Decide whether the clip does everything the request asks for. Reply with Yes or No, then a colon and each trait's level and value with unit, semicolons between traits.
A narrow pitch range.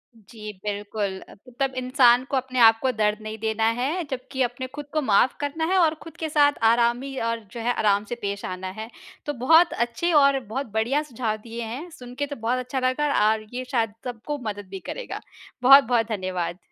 No: average, 4.0 semitones